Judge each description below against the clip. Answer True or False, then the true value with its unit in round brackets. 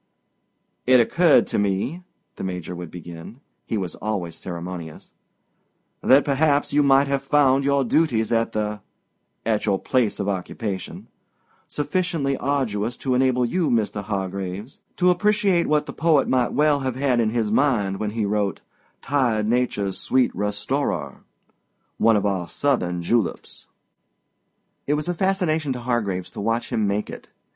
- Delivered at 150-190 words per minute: False (140 wpm)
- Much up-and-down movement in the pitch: True (5.7 semitones)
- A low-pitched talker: True (120 Hz)